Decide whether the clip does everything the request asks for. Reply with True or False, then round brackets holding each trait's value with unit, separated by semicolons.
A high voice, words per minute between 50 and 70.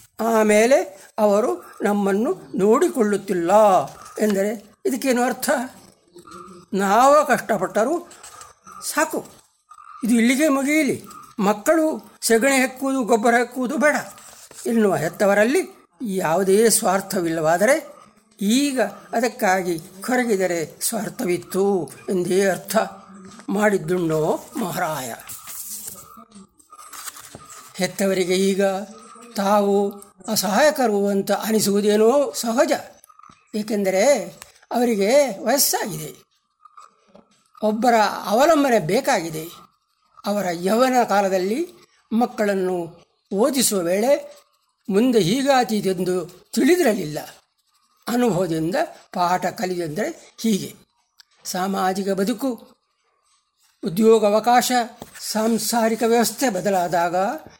True (220 Hz; 65 wpm)